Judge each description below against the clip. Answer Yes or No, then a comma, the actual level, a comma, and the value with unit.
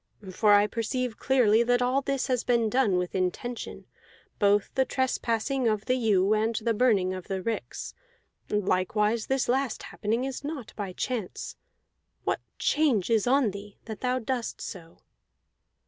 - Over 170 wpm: No, average, 155 wpm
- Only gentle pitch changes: No, average, 3.6 semitones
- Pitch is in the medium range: No, high, 230 Hz